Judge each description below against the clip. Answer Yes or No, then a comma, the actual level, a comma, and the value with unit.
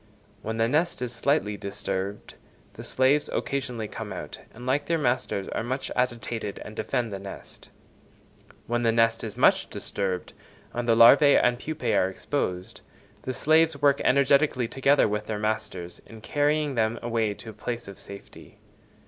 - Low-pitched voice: Yes, low, 115 Hz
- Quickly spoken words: No, average, 165 wpm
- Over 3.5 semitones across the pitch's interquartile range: Yes, average, 4.5 semitones